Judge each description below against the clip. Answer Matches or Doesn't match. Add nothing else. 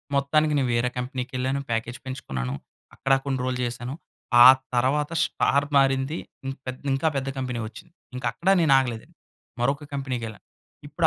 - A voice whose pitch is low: Matches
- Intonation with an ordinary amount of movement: Doesn't match